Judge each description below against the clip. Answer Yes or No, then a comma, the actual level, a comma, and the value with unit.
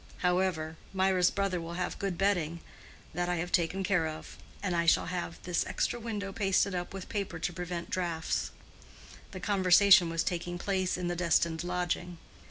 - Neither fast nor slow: Yes, average, 170 wpm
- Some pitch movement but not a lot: No, narrow, 2.0 semitones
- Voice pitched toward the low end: No, medium, 180 Hz